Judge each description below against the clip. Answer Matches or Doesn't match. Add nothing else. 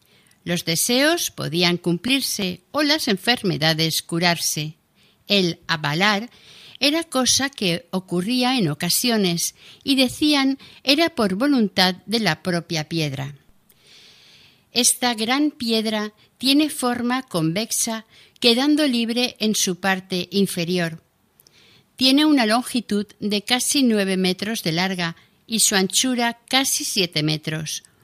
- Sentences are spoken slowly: Matches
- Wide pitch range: Matches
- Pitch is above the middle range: Matches